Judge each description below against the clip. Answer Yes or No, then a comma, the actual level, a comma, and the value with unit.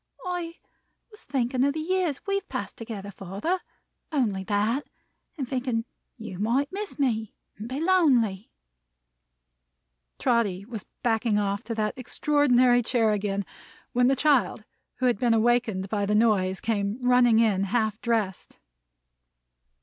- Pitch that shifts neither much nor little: Yes, average, 4.2 semitones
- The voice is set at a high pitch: Yes, high, 235 Hz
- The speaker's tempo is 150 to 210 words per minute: No, slow, 135 wpm